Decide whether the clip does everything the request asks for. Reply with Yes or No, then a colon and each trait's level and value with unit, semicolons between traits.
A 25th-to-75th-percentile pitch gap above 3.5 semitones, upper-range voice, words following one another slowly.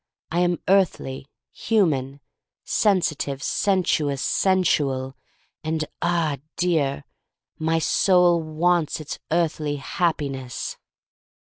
No: average, 3.9 semitones; medium, 160 Hz; slow, 95 wpm